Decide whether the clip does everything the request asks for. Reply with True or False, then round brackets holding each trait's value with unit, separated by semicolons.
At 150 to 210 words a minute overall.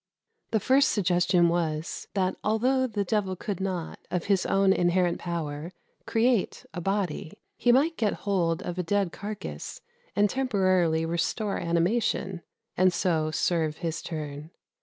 False (140 wpm)